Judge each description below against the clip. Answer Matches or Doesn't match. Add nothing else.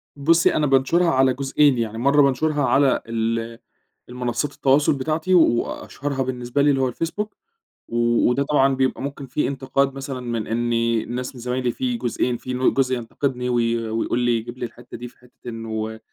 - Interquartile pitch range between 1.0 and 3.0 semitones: Matches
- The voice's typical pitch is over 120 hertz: Matches